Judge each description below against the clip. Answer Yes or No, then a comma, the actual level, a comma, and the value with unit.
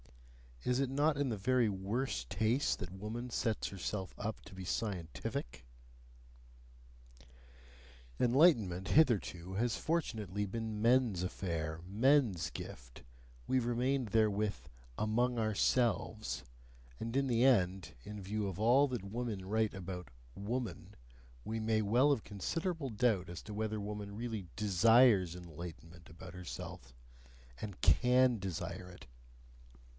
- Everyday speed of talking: No, slow, 125 wpm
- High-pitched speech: No, low, 105 Hz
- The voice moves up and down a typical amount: Yes, average, 4.5 semitones